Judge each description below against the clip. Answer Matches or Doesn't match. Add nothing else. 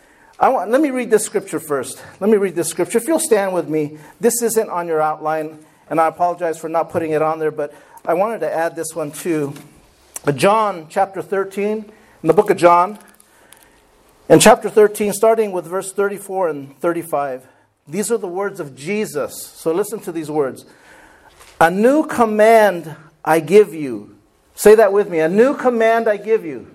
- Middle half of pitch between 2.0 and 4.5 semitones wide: Doesn't match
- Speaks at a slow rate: Doesn't match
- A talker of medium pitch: Matches